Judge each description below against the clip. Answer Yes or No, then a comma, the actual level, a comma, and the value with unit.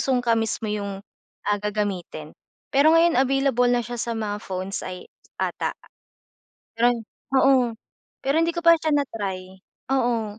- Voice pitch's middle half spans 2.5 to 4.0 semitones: No, average, 4.7 semitones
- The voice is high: Yes, high, 235 Hz